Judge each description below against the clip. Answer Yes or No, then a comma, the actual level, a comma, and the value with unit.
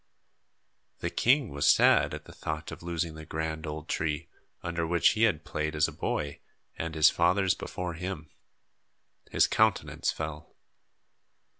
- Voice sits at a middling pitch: No, very low, 80 Hz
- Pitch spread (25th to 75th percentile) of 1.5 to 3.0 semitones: Yes, narrow, 2.4 semitones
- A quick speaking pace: No, average, 150 wpm